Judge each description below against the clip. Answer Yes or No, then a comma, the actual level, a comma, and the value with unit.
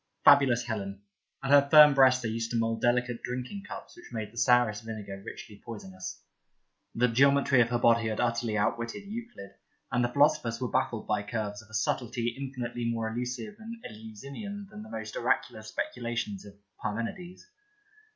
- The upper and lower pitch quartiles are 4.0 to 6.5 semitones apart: No, average, 3.6 semitones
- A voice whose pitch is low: Yes, low, 120 Hz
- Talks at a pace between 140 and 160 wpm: No, average, 170 wpm